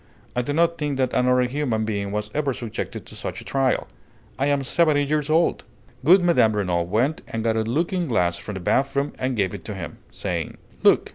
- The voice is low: Yes, low, 125 Hz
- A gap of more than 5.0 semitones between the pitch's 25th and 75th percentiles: Yes, wide, 5.5 semitones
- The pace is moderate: No, fast, 215 wpm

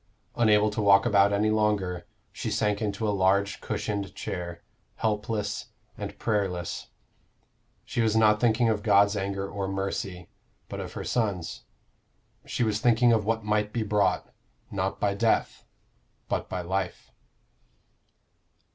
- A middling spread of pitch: No, narrow, 1.8 semitones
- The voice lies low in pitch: Yes, low, 105 Hz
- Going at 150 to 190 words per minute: No, average, 140 wpm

